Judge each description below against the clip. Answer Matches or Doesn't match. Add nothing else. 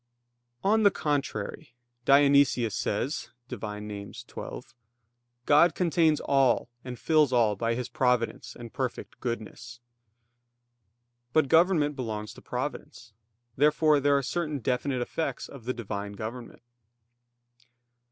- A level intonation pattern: Doesn't match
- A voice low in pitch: Matches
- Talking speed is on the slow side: Matches